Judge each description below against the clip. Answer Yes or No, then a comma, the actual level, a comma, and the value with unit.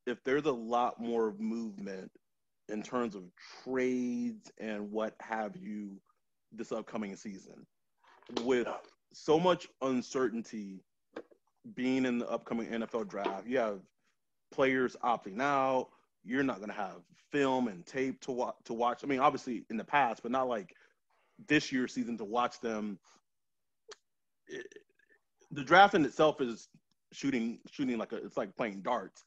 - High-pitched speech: No, low, 125 Hz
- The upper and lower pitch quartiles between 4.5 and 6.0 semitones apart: No, average, 4.1 semitones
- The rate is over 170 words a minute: No, average, 150 wpm